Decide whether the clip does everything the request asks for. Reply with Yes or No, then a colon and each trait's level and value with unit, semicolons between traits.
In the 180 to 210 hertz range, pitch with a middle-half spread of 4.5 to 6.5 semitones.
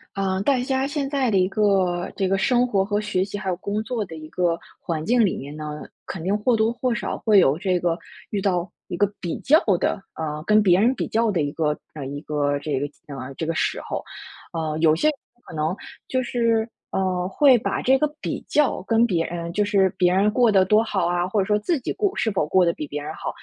Yes: high, 190 Hz; average, 5.0 semitones